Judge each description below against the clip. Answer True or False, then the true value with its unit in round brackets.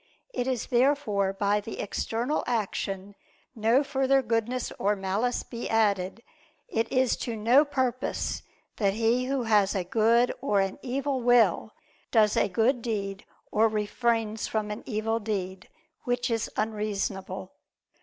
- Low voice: False (225 Hz)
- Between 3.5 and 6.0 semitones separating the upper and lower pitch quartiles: False (3.1 semitones)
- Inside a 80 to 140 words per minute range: True (135 wpm)